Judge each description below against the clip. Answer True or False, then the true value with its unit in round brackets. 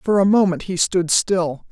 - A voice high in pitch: False (180 Hz)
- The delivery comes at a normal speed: False (210 wpm)